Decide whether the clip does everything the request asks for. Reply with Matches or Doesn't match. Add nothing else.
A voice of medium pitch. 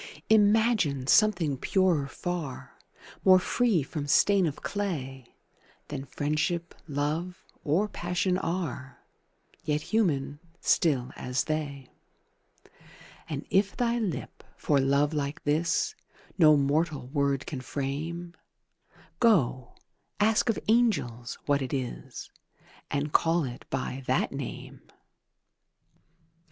Matches